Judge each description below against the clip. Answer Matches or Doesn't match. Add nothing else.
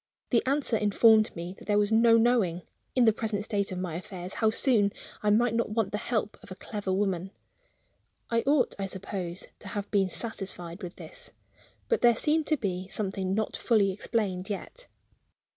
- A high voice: Matches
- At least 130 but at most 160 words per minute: Doesn't match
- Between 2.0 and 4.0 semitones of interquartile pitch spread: Matches